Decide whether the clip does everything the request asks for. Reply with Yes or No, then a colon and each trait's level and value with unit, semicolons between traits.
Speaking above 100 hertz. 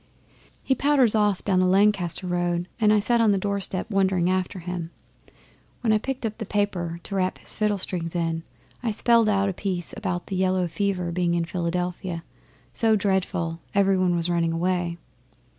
Yes: medium, 185 Hz